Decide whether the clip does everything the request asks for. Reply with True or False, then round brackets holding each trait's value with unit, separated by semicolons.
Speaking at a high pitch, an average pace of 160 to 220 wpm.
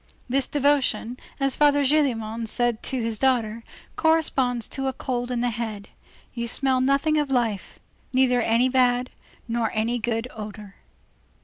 False (245 Hz; 145 wpm)